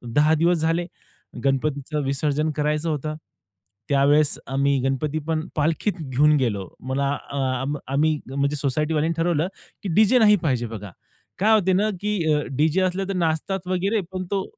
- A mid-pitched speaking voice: Yes, medium, 155 Hz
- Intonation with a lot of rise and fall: No, average, 3.9 semitones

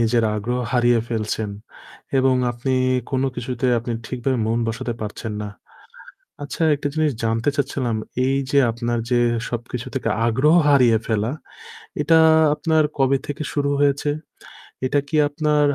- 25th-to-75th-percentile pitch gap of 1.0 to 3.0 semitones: No, average, 3.6 semitones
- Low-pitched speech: Yes, low, 125 Hz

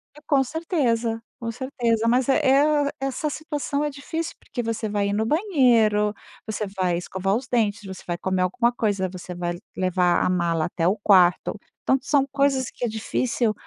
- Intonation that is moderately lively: No, wide, 6.0 semitones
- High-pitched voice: Yes, high, 230 Hz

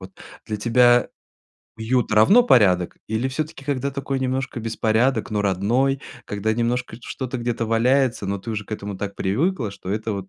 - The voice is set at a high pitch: No, low, 115 Hz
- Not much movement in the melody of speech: No, average, 3.8 semitones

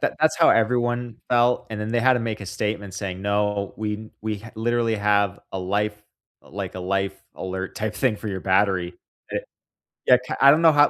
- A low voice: Yes, low, 105 Hz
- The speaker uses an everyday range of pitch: Yes, average, 3.0 semitones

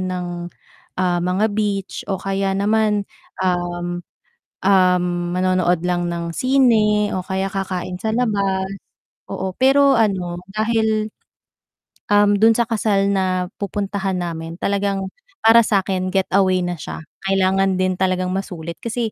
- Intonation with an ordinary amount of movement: No, narrow, 2.3 semitones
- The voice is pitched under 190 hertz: No, high, 195 Hz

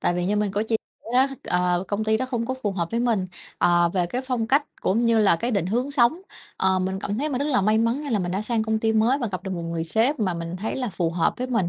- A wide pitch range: No, average, 4.7 semitones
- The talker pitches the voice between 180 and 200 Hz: No, high, 220 Hz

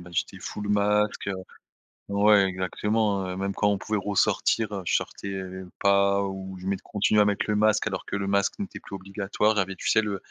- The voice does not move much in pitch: Yes, narrow, 1.4 semitones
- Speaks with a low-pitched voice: Yes, low, 100 Hz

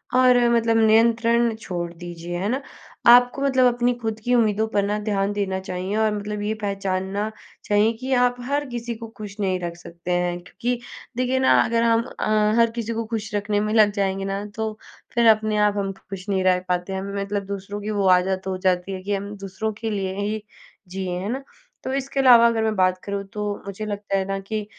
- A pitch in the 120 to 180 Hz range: No, high, 210 Hz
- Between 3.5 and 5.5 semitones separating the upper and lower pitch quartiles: No, average, 3.1 semitones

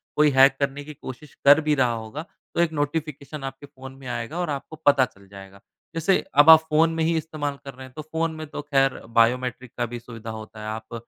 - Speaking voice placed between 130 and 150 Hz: Yes, medium, 140 Hz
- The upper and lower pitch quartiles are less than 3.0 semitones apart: No, average, 4.0 semitones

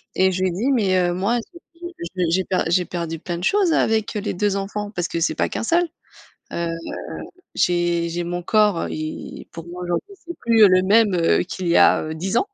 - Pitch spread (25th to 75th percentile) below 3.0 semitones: No, average, 3.5 semitones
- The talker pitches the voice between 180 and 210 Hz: Yes, medium, 185 Hz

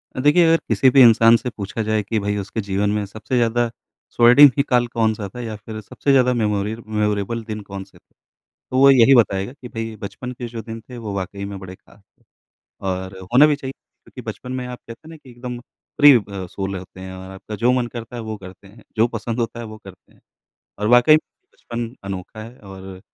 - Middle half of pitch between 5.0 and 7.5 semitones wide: No, average, 3.5 semitones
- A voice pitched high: No, low, 110 Hz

